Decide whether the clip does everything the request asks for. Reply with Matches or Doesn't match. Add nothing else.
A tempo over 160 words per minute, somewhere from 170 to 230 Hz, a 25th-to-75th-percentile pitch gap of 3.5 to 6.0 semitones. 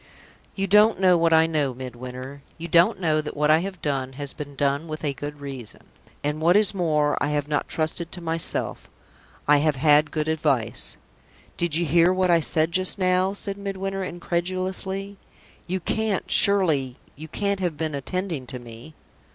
Doesn't match